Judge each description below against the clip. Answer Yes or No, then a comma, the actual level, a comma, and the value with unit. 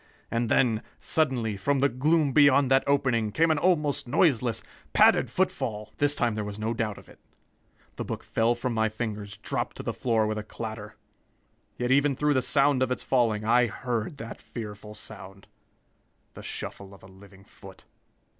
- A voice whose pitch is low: Yes, low, 120 Hz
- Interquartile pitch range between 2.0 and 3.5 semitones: No, average, 4.4 semitones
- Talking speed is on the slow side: No, average, 180 wpm